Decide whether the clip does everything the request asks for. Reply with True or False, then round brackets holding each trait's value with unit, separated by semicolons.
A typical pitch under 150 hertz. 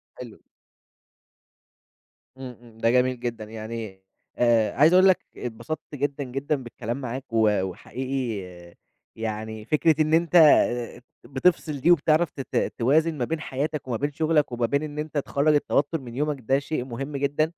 True (135 Hz)